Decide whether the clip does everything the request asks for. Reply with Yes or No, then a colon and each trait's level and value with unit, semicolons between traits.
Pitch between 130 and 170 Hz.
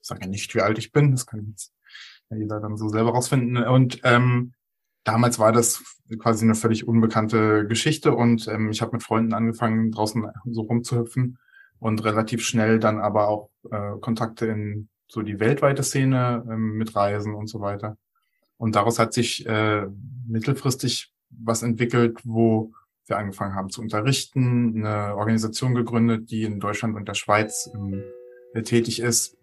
No: low, 115 Hz